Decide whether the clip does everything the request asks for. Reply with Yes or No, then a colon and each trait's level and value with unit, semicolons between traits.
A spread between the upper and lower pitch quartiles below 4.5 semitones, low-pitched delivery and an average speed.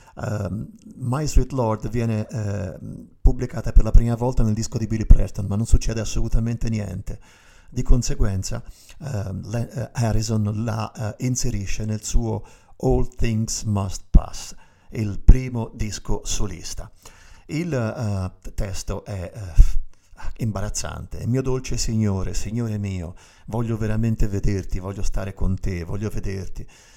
Yes: average, 2.9 semitones; low, 110 Hz; average, 135 wpm